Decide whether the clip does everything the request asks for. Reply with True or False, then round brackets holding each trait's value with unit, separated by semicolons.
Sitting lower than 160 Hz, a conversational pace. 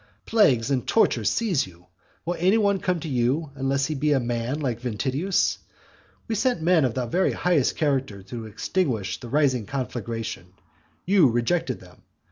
True (135 Hz; 165 wpm)